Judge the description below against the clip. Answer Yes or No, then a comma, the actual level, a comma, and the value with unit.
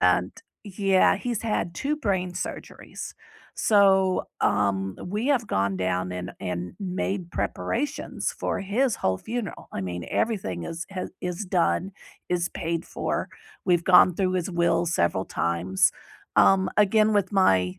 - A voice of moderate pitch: Yes, medium, 180 Hz